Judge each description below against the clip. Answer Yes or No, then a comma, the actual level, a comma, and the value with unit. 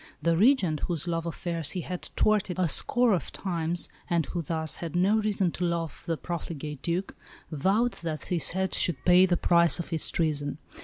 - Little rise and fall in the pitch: Yes, narrow, 2.2 semitones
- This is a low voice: No, medium, 170 Hz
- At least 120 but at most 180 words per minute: No, average, 190 wpm